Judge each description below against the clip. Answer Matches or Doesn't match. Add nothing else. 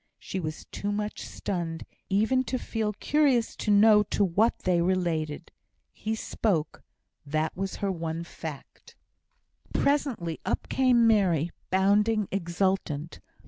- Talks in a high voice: Matches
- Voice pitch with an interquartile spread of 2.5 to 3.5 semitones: Doesn't match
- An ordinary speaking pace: Doesn't match